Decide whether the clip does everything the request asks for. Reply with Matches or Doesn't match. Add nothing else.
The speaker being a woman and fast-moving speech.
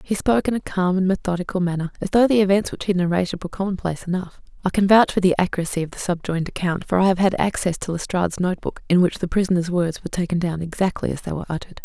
Matches